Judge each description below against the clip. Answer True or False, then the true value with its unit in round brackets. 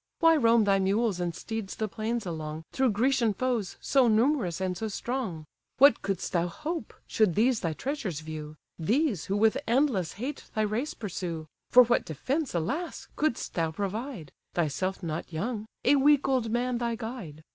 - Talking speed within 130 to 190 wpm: True (170 wpm)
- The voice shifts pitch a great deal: True (6.2 semitones)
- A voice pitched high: True (220 Hz)